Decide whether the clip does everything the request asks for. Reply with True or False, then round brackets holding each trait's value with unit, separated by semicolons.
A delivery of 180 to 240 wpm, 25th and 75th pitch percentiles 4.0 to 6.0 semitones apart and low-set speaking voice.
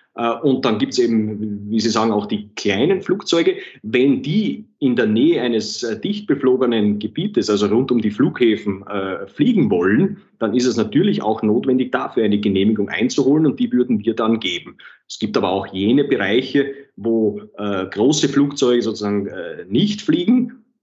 False (160 wpm; 5.1 semitones; 115 Hz)